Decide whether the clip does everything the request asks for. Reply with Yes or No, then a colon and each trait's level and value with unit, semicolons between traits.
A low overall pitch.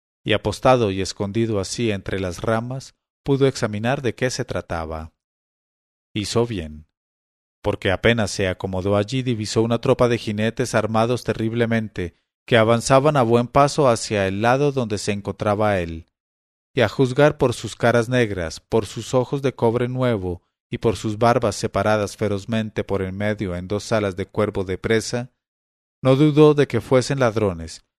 Yes: low, 110 Hz